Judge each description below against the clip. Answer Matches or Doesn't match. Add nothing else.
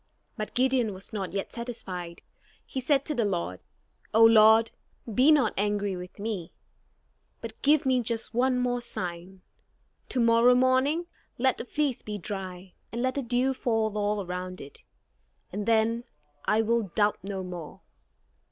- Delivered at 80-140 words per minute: Doesn't match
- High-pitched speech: Matches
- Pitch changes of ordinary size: Matches